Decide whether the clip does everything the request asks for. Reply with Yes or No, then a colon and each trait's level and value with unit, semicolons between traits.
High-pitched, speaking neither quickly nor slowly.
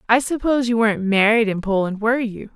No: high, 225 Hz; fast, 210 wpm